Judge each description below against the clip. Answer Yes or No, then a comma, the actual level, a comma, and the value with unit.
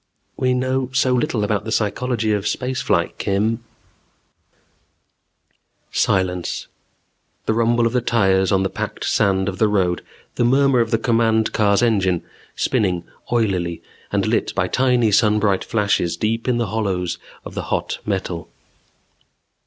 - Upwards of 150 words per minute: No, average, 145 wpm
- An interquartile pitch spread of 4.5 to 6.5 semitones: No, average, 3.7 semitones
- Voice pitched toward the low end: Yes, low, 110 Hz